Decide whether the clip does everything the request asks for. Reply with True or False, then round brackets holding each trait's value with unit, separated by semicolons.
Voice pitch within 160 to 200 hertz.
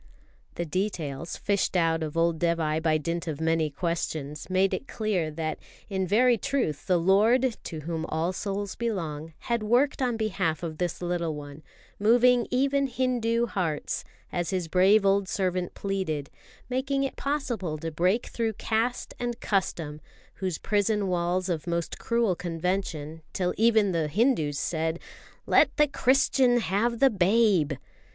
True (185 Hz)